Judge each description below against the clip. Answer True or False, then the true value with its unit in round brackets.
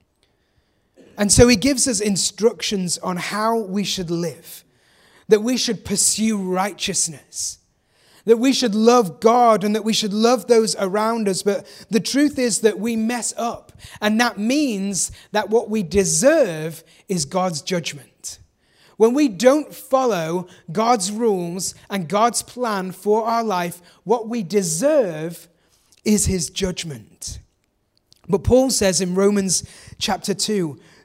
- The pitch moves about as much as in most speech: True (3.9 semitones)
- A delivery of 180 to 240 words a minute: False (140 wpm)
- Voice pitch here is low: False (210 Hz)